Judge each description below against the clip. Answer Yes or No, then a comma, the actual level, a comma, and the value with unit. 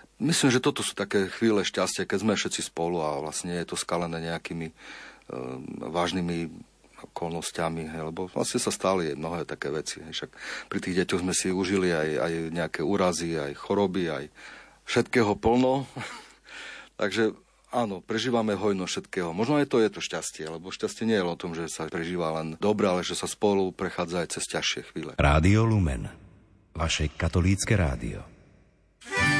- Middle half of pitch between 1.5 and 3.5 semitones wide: No, average, 4.1 semitones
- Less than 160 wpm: No, fast, 165 wpm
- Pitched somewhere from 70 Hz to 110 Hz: Yes, very low, 90 Hz